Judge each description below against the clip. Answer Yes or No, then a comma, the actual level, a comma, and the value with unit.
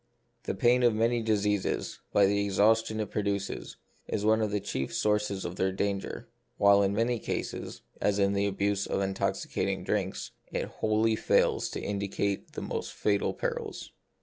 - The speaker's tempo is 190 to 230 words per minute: No, average, 170 wpm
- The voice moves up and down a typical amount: No, narrow, 1.6 semitones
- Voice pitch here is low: Yes, low, 100 Hz